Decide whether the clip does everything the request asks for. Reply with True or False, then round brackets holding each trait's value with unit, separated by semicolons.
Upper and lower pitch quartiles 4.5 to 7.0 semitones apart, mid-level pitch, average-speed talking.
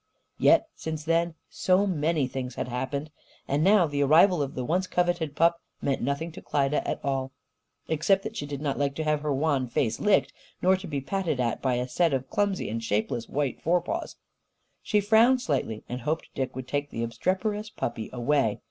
True (5.0 semitones; 150 Hz; 195 wpm)